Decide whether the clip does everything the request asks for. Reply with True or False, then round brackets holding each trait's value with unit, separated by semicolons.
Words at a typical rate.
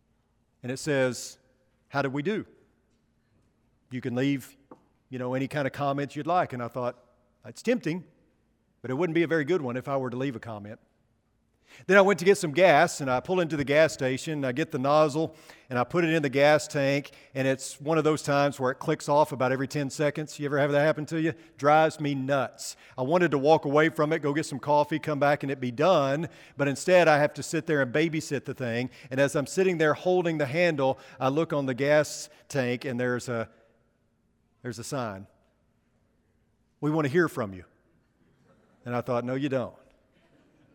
False (220 wpm)